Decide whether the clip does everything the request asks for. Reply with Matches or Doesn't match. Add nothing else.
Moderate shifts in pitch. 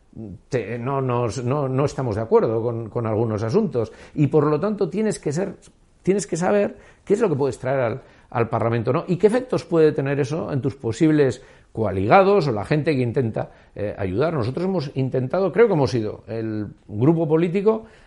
Doesn't match